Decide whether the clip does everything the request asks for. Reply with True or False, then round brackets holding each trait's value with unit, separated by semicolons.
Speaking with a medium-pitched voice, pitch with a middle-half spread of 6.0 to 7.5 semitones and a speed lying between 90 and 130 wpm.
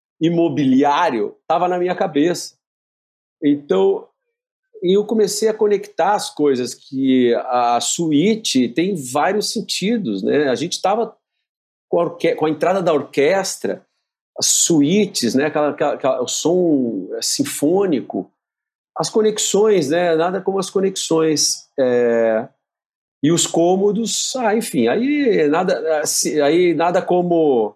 True (175 Hz; 6.5 semitones; 120 wpm)